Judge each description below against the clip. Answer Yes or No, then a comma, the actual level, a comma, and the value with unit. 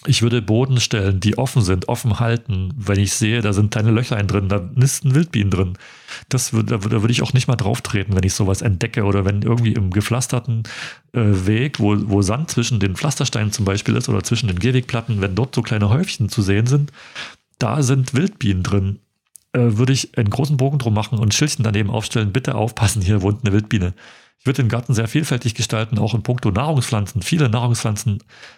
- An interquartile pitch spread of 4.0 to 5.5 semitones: No, average, 3.4 semitones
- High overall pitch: No, low, 115 Hz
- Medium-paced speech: No, fast, 205 wpm